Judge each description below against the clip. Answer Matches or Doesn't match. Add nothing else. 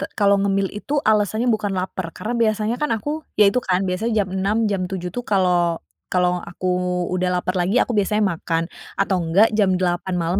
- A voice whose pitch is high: Matches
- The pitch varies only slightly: Doesn't match